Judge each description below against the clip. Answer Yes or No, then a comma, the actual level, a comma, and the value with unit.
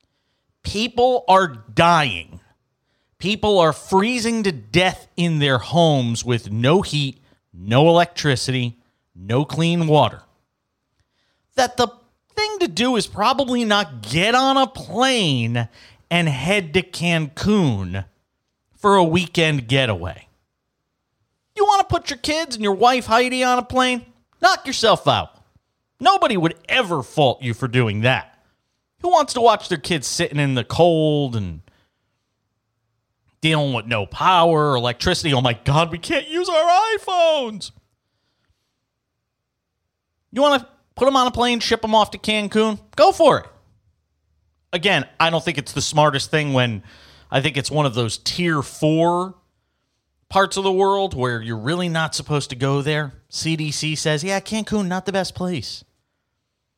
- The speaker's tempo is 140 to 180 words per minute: Yes, average, 150 wpm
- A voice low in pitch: No, medium, 155 Hz